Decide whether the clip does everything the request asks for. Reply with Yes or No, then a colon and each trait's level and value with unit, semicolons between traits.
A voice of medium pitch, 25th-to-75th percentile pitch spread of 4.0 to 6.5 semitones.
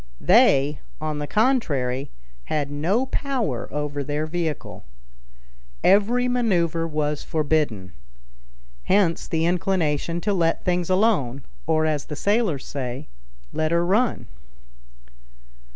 Yes: medium, 160 Hz; average, 5.1 semitones